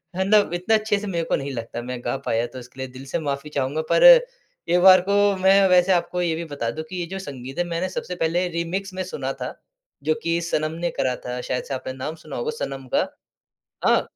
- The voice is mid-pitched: Yes, medium, 165 Hz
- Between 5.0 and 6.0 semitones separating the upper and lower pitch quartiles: Yes, wide, 5.4 semitones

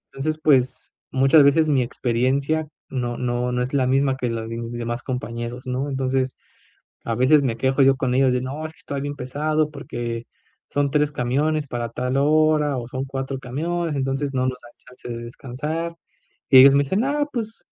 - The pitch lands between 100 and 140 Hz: Yes, low, 135 Hz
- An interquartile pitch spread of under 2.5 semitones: No, average, 2.8 semitones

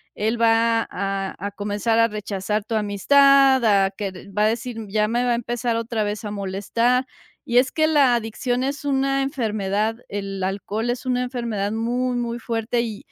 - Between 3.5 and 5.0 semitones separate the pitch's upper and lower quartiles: No, average, 3.1 semitones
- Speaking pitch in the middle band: No, high, 225 Hz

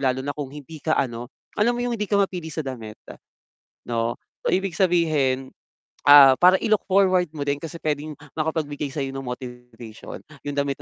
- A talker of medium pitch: Yes, medium, 145 Hz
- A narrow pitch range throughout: No, average, 4.4 semitones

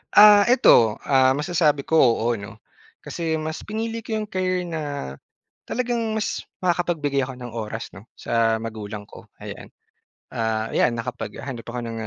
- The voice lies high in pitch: No, low, 135 Hz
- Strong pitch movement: Yes, wide, 8.0 semitones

